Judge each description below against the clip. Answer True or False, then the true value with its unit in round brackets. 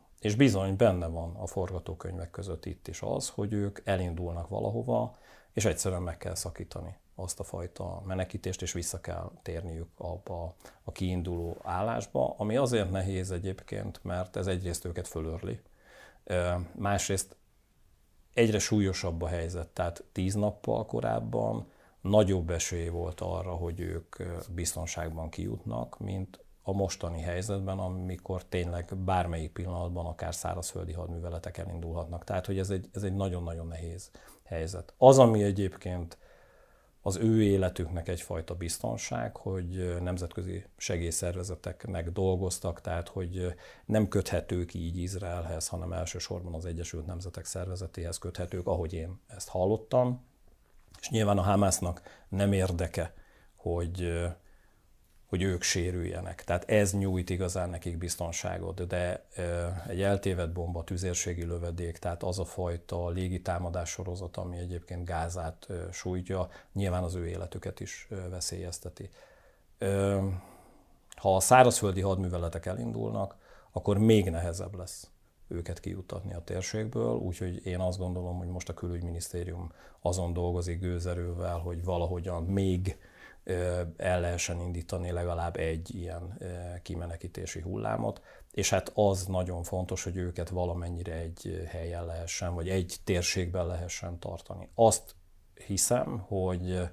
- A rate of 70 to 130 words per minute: True (125 wpm)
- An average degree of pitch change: False (1.8 semitones)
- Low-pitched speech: True (90 Hz)